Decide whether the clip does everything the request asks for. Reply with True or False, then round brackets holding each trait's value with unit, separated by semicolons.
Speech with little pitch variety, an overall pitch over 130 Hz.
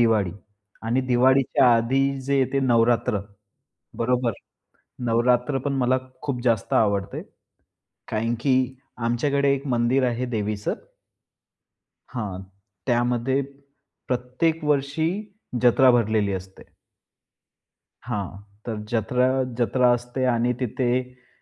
False (2.3 semitones; 125 Hz)